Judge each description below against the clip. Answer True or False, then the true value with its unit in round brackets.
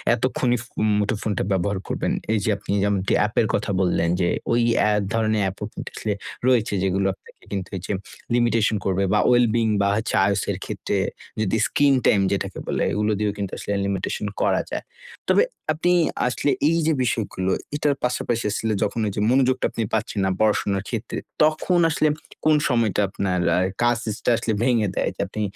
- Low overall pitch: True (110 Hz)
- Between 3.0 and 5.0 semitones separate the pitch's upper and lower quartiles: True (3.3 semitones)